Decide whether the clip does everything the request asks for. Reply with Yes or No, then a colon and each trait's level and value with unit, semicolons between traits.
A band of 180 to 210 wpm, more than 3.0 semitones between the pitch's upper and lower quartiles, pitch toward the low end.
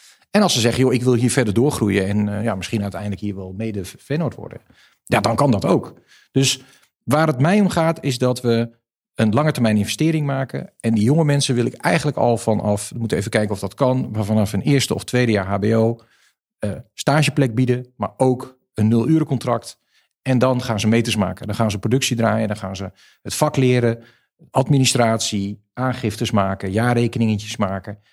Yes: fast, 200 wpm; average, 3.6 semitones; low, 115 Hz